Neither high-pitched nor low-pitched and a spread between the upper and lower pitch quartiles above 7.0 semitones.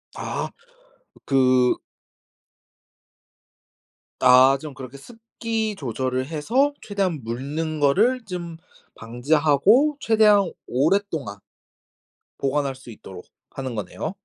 Yes: medium, 150 Hz; wide, 7.8 semitones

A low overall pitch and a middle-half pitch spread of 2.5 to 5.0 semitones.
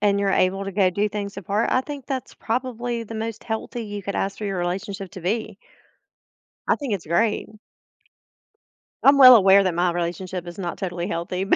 No: high, 200 Hz; average, 3.4 semitones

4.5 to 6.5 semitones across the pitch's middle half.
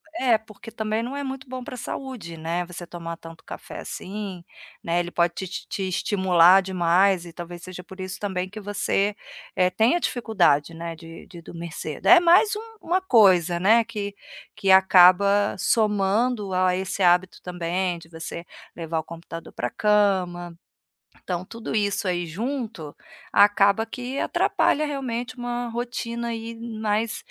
Yes: average, 4.8 semitones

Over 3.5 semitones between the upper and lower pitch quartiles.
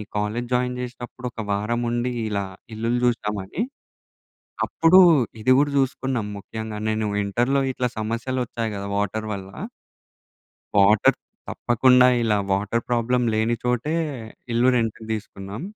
No: average, 2.7 semitones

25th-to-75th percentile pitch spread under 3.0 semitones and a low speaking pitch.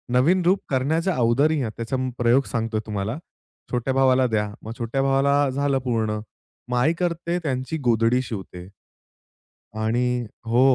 No: average, 3.6 semitones; low, 125 Hz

